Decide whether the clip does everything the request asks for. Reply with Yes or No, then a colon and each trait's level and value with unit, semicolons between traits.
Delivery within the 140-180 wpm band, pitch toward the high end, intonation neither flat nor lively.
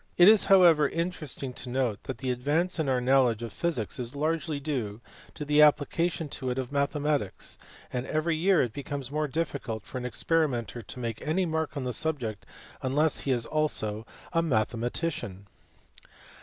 No: average, 170 wpm; medium, 140 Hz; average, 4.4 semitones